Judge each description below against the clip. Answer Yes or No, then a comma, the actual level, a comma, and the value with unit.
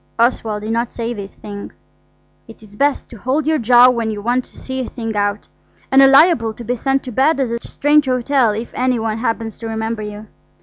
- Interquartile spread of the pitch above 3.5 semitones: No, average, 2.9 semitones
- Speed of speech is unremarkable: No, fast, 225 wpm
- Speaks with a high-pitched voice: Yes, high, 235 Hz